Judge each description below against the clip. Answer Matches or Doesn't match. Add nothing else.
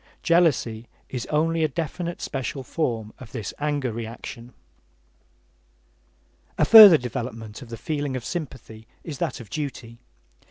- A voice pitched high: Doesn't match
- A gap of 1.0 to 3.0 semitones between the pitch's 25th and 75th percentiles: Doesn't match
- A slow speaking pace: Matches